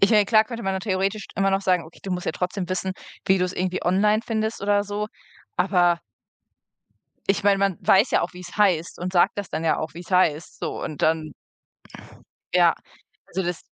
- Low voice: No, high, 190 Hz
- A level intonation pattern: Yes, narrow, 2.3 semitones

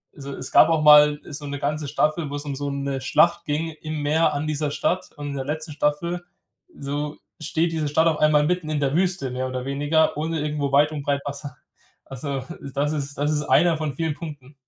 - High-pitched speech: No, medium, 150 Hz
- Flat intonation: Yes, narrow, 1.7 semitones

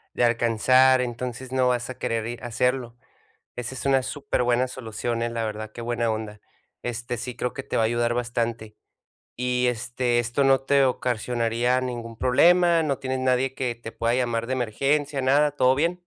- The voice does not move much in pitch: Yes, narrow, 1.9 semitones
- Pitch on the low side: Yes, low, 125 Hz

